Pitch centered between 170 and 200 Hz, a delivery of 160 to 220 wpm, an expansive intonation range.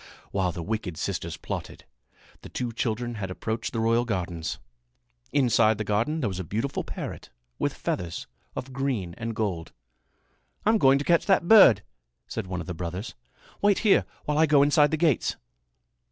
No: low, 115 Hz; average, 170 wpm; wide, 6.9 semitones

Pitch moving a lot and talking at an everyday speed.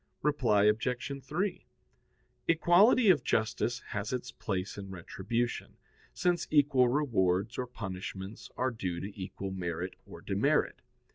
No: wide, 6.3 semitones; slow, 125 wpm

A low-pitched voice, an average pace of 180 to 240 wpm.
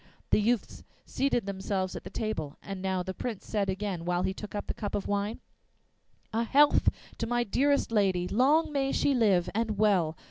No: high, 205 Hz; average, 190 wpm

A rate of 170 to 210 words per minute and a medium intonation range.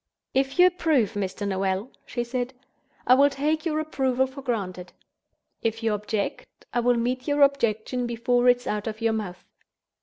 Yes: average, 175 wpm; average, 3.9 semitones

